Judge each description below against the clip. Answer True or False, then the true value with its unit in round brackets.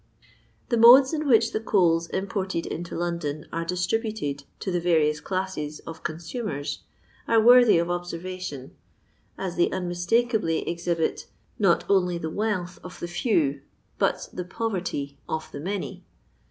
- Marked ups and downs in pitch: False (4.1 semitones)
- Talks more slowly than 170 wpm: True (140 wpm)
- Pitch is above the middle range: False (175 Hz)